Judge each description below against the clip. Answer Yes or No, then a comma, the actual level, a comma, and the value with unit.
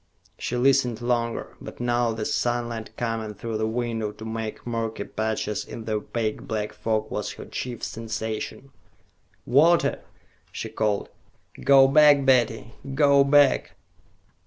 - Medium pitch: No, low, 115 Hz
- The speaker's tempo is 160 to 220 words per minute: No, slow, 135 wpm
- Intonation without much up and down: Yes, narrow, 2.3 semitones